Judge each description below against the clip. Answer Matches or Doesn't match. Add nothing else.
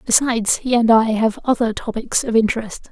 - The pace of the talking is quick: Doesn't match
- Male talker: Doesn't match